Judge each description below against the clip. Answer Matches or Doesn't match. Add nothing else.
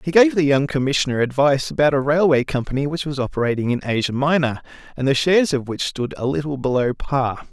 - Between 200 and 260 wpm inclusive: Matches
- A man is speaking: Matches